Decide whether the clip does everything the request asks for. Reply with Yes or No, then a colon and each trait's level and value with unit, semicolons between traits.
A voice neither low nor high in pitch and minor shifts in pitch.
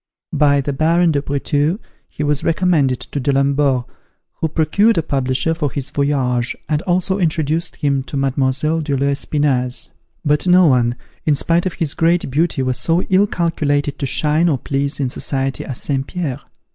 No: medium, 145 Hz; average, 3.2 semitones